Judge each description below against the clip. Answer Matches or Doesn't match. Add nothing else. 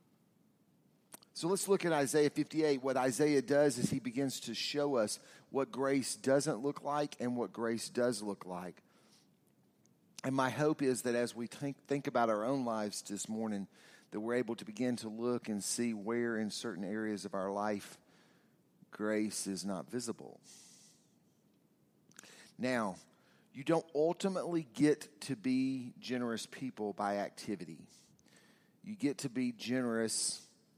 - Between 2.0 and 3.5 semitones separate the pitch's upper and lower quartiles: Doesn't match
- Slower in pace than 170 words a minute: Matches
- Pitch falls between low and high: Doesn't match